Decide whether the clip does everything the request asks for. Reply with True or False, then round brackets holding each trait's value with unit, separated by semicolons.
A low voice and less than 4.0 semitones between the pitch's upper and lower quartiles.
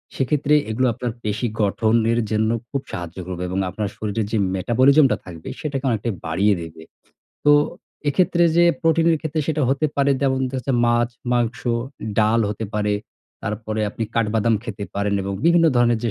False (115 Hz; 4.7 semitones)